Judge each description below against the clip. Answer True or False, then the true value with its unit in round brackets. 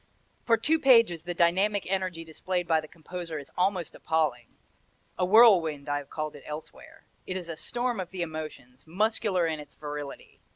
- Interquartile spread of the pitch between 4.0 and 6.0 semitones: False (3.6 semitones)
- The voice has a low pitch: False (170 Hz)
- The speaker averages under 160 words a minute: False (175 wpm)